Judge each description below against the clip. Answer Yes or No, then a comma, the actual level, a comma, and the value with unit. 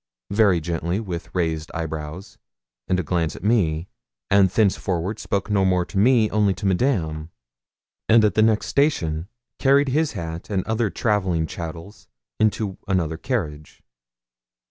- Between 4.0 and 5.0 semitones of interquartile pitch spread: Yes, average, 4.7 semitones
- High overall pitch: No, very low, 95 Hz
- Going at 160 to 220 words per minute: No, average, 145 wpm